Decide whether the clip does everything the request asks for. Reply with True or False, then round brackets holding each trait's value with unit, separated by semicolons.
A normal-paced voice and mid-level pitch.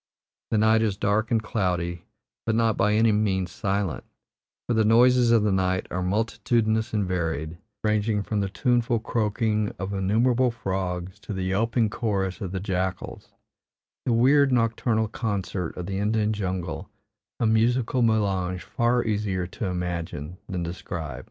False (150 wpm; 105 Hz)